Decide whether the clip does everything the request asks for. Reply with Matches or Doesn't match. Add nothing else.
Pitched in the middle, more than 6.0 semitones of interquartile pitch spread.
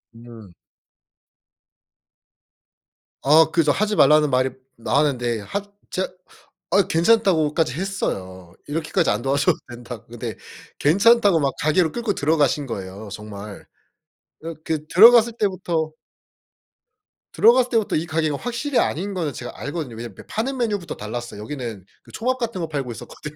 Matches